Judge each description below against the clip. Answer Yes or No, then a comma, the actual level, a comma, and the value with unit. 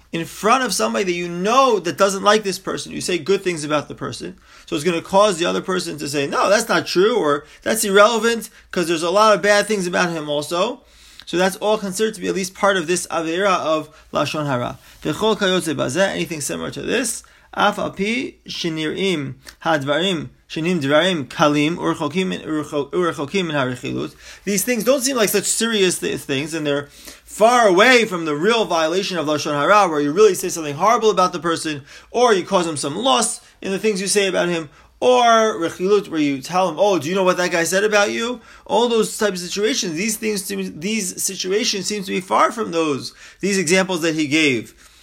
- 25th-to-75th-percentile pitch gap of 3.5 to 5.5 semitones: Yes, average, 4.3 semitones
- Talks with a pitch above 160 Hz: Yes, medium, 185 Hz